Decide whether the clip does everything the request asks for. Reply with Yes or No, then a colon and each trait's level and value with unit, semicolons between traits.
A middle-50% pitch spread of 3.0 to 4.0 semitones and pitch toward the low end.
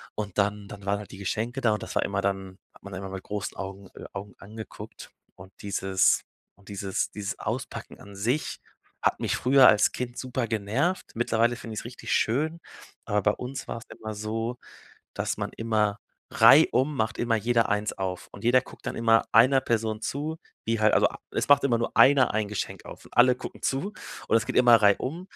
Yes: average, 3.4 semitones; low, 110 Hz